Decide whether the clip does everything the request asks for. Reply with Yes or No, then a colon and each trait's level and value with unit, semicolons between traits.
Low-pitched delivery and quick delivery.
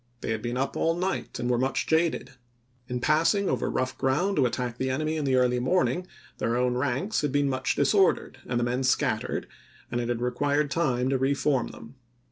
Yes: low, 130 Hz; fast, 215 wpm